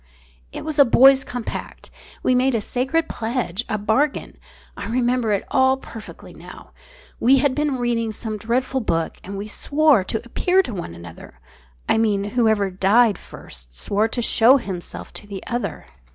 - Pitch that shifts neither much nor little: Yes, average, 4.2 semitones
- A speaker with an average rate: Yes, average, 165 wpm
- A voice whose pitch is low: No, high, 230 Hz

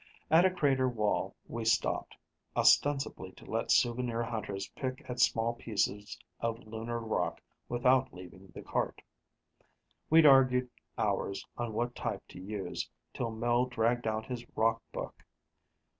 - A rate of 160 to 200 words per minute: No, average, 140 wpm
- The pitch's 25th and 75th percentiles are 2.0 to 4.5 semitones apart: Yes, narrow, 2.4 semitones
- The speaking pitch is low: Yes, low, 120 Hz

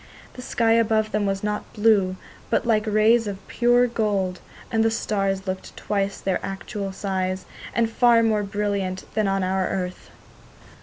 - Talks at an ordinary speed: Yes, average, 160 wpm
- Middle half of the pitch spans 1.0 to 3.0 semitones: Yes, narrow, 2.6 semitones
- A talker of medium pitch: No, high, 210 Hz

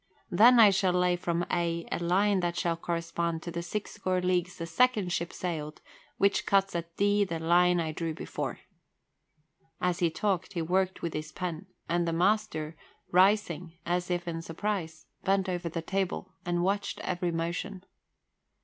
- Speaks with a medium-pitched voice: Yes, medium, 175 Hz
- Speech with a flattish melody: Yes, narrow, 2.3 semitones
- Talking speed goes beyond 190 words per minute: No, average, 170 wpm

